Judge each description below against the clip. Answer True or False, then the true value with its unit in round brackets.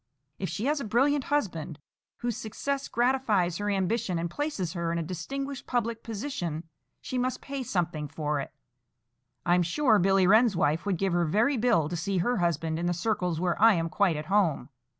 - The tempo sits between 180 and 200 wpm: True (190 wpm)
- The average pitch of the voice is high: True (195 Hz)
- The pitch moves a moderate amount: False (5.9 semitones)